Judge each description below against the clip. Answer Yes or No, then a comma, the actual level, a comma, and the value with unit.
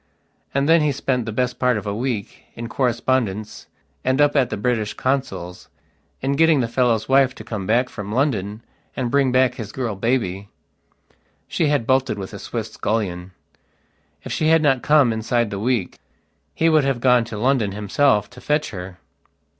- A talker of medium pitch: No, low, 125 Hz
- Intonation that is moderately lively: Yes, average, 4.0 semitones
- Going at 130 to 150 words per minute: No, average, 180 wpm